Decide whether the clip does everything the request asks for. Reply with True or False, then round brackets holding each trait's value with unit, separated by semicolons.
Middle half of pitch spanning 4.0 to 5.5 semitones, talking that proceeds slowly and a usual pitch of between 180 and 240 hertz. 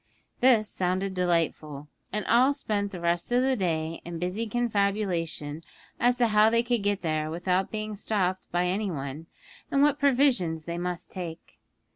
False (4.7 semitones; 165 wpm; 190 Hz)